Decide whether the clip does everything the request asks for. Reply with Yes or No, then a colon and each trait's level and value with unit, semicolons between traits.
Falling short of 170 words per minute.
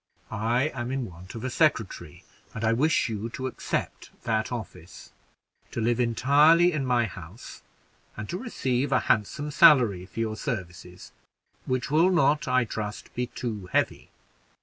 Yes: average, 155 wpm